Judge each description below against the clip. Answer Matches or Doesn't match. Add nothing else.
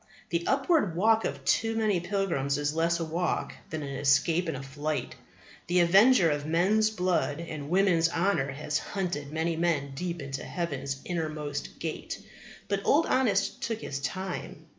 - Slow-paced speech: Doesn't match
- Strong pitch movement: Doesn't match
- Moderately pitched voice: Matches